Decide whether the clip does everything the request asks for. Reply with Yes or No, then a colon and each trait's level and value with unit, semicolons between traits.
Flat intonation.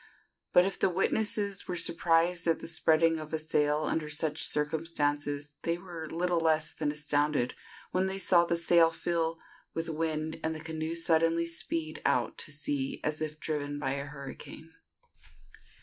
Yes: narrow, 1.9 semitones